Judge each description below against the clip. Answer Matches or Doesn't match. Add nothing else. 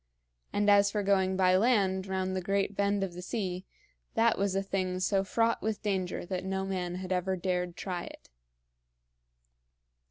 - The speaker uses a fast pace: Doesn't match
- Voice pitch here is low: Doesn't match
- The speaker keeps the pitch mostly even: Matches